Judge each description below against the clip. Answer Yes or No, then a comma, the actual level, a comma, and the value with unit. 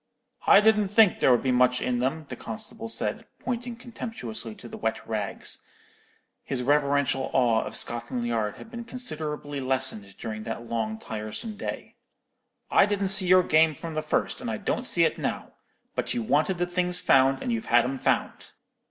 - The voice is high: No, medium, 140 Hz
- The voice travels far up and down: Yes, wide, 8.8 semitones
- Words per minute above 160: Yes, average, 185 wpm